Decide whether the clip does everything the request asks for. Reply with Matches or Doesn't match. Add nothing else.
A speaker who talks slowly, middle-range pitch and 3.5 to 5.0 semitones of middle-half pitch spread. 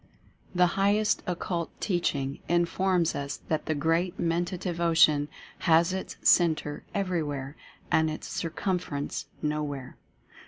Doesn't match